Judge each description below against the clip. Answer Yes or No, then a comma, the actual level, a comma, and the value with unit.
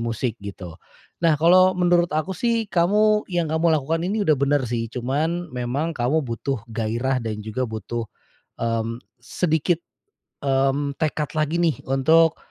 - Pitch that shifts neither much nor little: No, wide, 5.9 semitones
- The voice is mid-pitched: Yes, medium, 145 Hz